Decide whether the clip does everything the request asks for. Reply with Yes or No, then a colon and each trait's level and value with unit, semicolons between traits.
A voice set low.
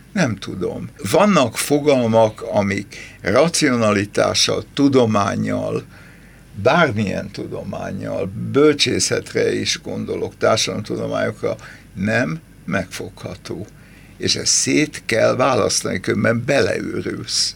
Yes: low, 115 Hz